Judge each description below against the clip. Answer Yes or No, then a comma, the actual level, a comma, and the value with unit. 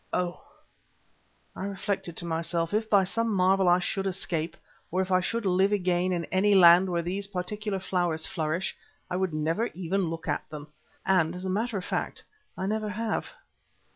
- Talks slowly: No, average, 180 wpm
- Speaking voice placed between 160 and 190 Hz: Yes, medium, 185 Hz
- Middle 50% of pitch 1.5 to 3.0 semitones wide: Yes, narrow, 2.5 semitones